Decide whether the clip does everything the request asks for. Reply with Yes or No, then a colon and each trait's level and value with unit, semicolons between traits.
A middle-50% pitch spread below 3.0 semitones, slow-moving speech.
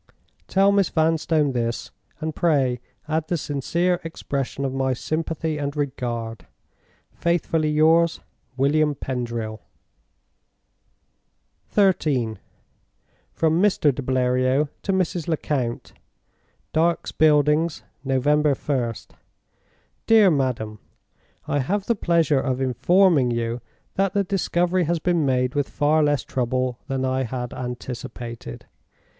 No: average, 4.3 semitones; slow, 110 wpm